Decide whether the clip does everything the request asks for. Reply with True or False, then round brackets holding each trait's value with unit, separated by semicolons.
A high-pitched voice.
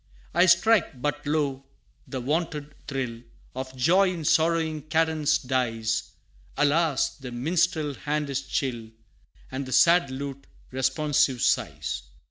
False (145 Hz)